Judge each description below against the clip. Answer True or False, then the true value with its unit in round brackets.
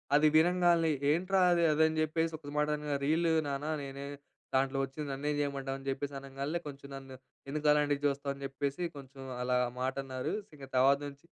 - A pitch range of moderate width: False (2.0 semitones)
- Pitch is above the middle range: False (140 Hz)